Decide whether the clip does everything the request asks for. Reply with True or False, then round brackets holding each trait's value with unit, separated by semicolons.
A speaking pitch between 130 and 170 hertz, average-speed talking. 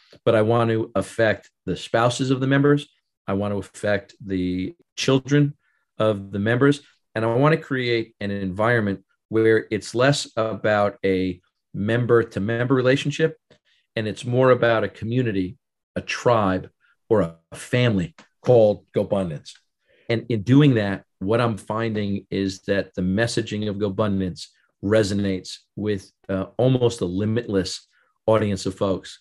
False (110 Hz; 145 wpm)